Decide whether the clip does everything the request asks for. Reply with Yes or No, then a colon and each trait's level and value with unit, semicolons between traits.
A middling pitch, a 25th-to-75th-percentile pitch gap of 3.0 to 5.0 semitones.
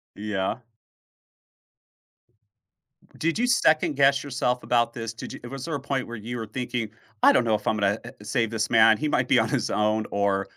No: low, 115 Hz; average, 3.7 semitones